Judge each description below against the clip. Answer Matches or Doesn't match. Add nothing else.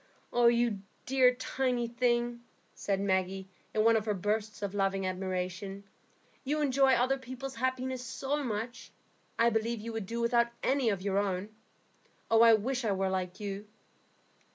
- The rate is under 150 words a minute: Doesn't match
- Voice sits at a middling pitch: Doesn't match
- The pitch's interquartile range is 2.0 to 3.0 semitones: Doesn't match